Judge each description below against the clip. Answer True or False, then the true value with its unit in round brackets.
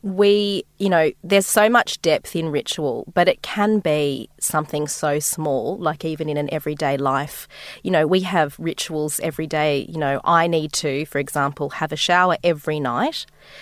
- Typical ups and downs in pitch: True (3.2 semitones)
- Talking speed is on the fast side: False (180 wpm)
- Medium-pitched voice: True (155 Hz)